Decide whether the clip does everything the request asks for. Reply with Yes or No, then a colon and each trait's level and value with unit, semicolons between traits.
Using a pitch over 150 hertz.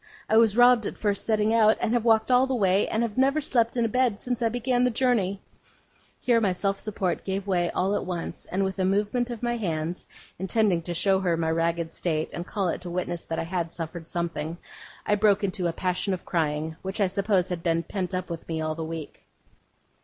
Yes: high, 190 Hz